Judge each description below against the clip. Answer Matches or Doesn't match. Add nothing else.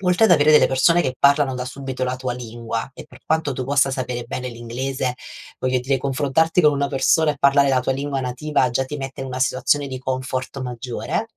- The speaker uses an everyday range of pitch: Doesn't match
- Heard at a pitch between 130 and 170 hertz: Matches